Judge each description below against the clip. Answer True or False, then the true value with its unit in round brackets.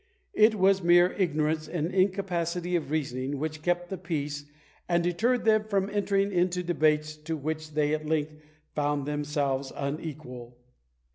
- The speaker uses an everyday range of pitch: True (3.3 semitones)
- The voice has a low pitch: False (160 Hz)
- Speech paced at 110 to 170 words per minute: True (145 wpm)